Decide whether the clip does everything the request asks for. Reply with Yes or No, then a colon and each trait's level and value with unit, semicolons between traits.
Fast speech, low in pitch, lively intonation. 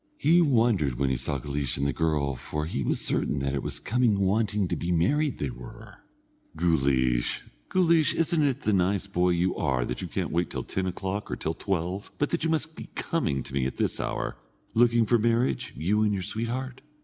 Yes: fast, 210 wpm; very low, 95 Hz; wide, 8.8 semitones